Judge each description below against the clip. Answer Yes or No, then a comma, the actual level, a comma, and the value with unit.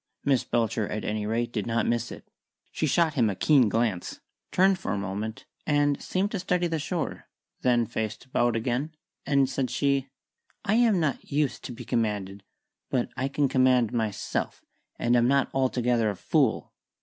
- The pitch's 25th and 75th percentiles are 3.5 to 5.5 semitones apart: Yes, average, 4.5 semitones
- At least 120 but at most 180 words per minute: Yes, average, 175 wpm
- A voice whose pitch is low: Yes, low, 125 Hz